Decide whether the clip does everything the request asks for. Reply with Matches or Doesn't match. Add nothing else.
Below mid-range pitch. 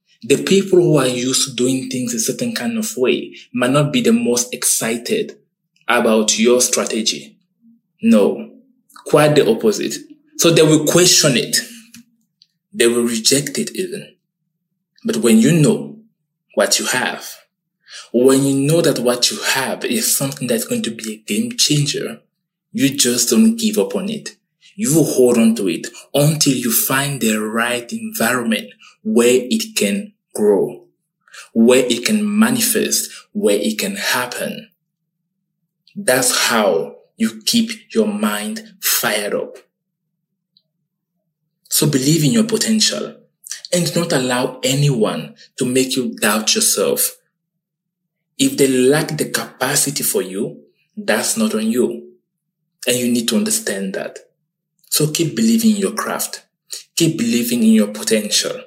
Doesn't match